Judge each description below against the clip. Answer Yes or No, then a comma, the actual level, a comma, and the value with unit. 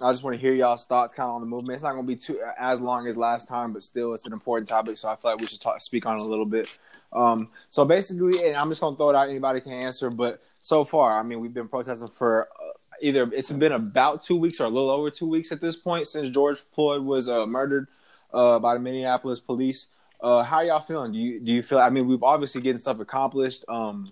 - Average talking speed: No, fast, 270 wpm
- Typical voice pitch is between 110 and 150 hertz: Yes, low, 130 Hz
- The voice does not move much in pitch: No, average, 3.2 semitones